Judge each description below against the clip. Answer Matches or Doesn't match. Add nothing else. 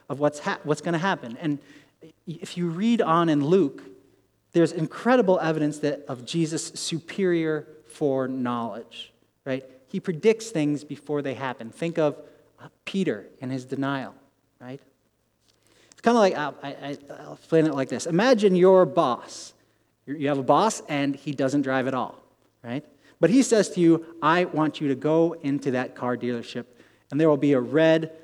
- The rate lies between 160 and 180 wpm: Matches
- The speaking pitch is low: Doesn't match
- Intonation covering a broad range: Doesn't match